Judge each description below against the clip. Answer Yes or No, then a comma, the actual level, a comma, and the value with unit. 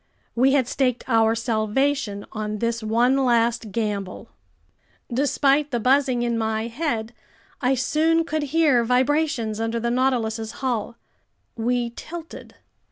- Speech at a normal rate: No, slow, 125 wpm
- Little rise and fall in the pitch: No, average, 3.3 semitones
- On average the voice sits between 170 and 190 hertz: No, high, 240 Hz